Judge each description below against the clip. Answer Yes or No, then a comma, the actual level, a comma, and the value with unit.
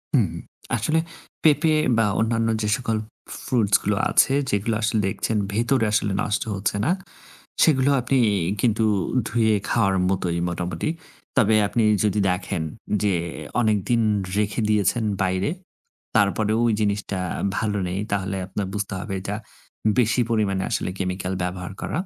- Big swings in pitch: No, average, 2.9 semitones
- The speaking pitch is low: Yes, low, 105 Hz